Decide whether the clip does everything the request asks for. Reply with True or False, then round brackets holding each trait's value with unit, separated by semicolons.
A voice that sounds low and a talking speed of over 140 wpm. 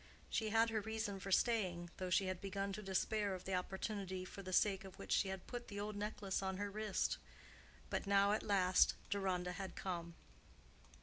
False (195 Hz; 195 wpm)